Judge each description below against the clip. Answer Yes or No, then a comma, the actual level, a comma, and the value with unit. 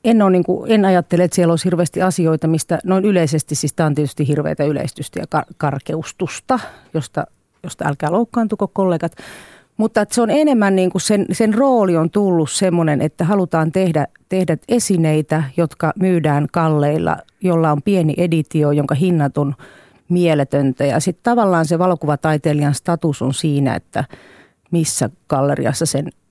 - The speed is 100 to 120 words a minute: No, fast, 155 wpm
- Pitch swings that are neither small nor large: Yes, average, 3.8 semitones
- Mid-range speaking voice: Yes, medium, 165 Hz